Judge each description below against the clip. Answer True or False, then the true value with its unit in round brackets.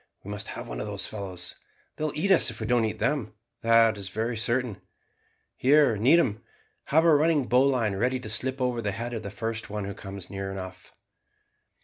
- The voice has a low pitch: True (115 Hz)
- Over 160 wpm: True (200 wpm)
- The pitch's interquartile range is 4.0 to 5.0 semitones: True (4.3 semitones)